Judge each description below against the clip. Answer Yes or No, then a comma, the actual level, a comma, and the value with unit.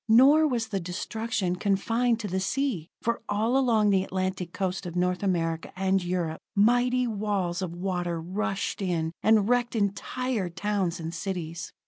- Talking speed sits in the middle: Yes, average, 155 wpm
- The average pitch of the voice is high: Yes, high, 195 Hz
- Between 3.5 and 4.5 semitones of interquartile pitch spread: Yes, average, 4.0 semitones